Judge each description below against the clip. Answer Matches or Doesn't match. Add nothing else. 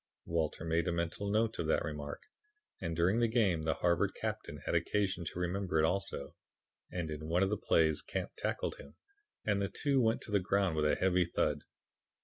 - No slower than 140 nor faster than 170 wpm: Doesn't match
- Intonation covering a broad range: Doesn't match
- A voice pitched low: Matches